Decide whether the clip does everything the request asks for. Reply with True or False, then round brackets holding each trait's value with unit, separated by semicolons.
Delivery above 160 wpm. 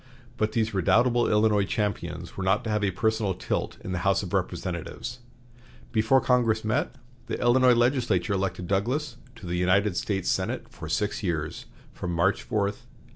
True (170 wpm)